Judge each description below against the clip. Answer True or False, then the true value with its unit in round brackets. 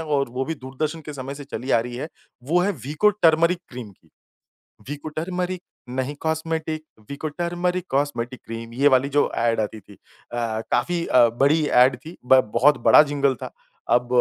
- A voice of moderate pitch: True (145 Hz)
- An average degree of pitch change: True (4.5 semitones)